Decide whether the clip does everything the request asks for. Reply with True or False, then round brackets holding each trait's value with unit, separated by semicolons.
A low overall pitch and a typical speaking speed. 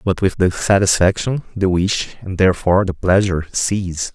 True (95 Hz; 160 wpm)